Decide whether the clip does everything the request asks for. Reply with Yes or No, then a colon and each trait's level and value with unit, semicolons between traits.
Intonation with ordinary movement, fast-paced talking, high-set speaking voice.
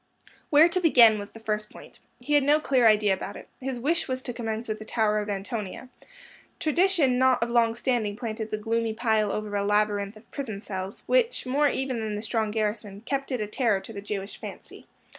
Yes: average, 3.6 semitones; fast, 215 wpm; high, 225 Hz